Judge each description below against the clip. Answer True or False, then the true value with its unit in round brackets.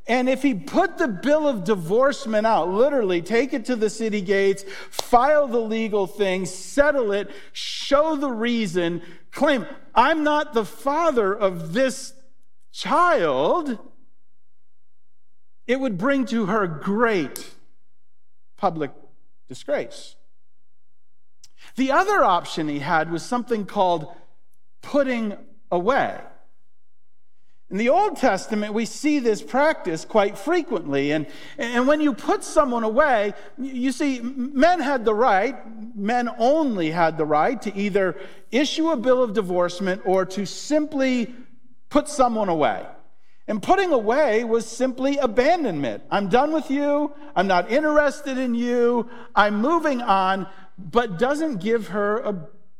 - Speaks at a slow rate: True (130 wpm)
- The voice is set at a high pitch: True (235 Hz)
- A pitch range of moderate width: False (5.9 semitones)